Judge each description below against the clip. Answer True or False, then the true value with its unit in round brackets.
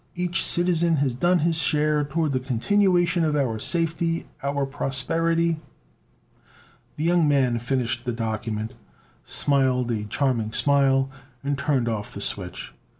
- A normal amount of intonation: True (4.8 semitones)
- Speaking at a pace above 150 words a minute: False (135 wpm)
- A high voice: False (140 Hz)